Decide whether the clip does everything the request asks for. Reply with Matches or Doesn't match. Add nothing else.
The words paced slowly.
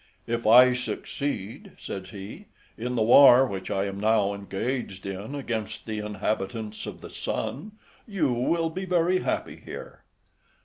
Doesn't match